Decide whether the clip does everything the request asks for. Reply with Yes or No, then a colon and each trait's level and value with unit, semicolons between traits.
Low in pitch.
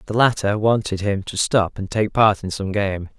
Yes: low, 105 Hz